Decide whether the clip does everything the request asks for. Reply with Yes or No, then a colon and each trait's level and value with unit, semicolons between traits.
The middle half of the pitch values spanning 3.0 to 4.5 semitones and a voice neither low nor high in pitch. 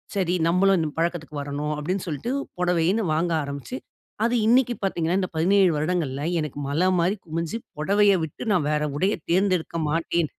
Yes: average, 3.9 semitones; medium, 170 Hz